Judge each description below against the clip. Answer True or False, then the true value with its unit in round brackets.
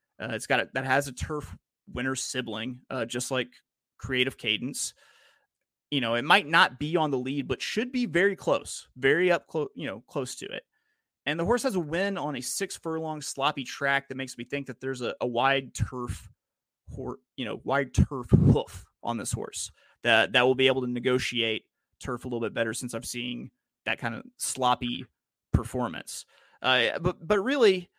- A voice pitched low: True (130 Hz)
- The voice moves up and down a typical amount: True (4.0 semitones)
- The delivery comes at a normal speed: True (195 wpm)